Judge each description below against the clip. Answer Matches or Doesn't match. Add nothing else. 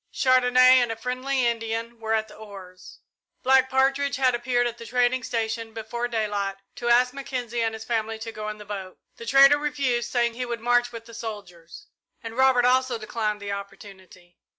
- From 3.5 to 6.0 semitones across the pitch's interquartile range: Doesn't match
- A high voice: Matches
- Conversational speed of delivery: Matches